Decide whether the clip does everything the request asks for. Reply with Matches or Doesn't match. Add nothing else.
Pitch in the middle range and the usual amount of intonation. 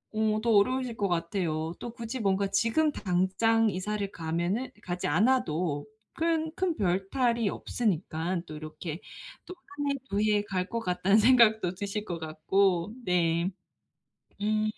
Doesn't match